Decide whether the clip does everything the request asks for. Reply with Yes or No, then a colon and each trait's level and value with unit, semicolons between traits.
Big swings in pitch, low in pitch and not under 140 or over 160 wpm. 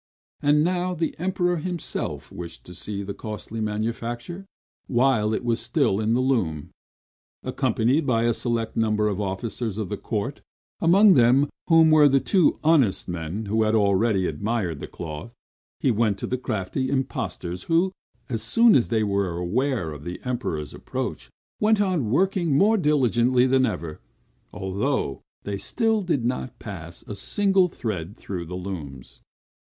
Yes: wide, 6.6 semitones; low, 115 Hz; average, 155 wpm